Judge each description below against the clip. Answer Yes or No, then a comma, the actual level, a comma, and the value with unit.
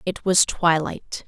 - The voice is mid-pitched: Yes, medium, 170 Hz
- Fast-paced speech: No, average, 140 wpm